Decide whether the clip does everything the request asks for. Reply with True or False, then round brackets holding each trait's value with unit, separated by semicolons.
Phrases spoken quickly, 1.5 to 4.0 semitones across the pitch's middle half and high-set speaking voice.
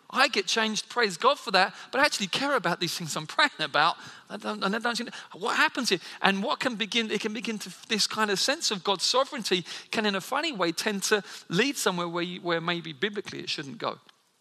False (235 wpm; 4.5 semitones; 210 Hz)